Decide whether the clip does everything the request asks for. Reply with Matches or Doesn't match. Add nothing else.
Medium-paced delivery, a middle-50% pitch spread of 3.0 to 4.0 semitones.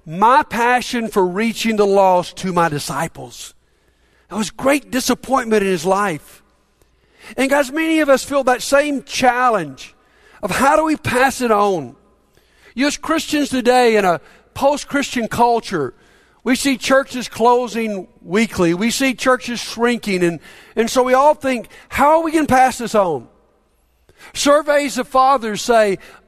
Doesn't match